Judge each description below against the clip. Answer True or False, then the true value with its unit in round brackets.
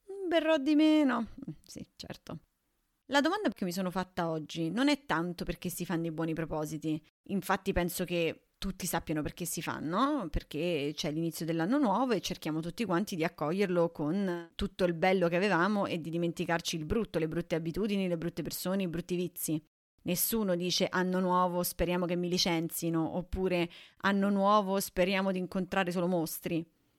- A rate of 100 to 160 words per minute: False (170 wpm)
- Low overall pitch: False (175 Hz)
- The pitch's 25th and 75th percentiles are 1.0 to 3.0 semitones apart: True (2.5 semitones)